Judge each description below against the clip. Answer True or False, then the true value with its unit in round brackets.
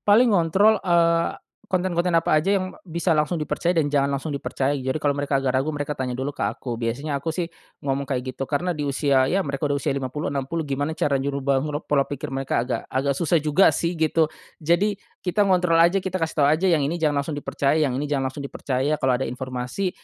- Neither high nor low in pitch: True (150 Hz)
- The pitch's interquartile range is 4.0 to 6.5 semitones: False (3.6 semitones)